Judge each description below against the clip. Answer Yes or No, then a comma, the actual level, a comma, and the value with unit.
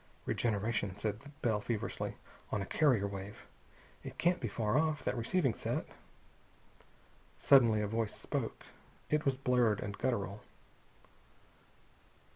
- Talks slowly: Yes, slow, 120 wpm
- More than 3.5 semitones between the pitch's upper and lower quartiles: Yes, average, 4.0 semitones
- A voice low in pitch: Yes, low, 115 Hz